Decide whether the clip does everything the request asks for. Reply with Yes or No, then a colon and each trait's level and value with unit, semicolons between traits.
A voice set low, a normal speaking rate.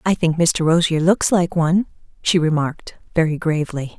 No: medium, 165 Hz; average, 165 wpm